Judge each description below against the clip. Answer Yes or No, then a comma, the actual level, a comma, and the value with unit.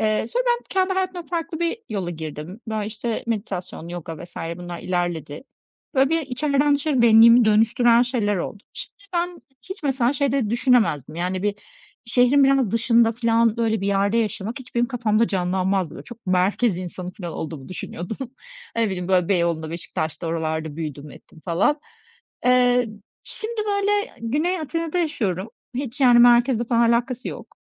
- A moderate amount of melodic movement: No, wide, 6.2 semitones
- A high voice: Yes, high, 230 Hz